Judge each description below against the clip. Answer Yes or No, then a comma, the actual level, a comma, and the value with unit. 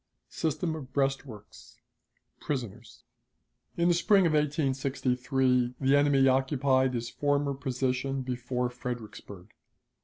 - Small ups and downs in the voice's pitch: Yes, narrow, 2.3 semitones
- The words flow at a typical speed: No, slow, 100 wpm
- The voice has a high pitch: No, low, 135 Hz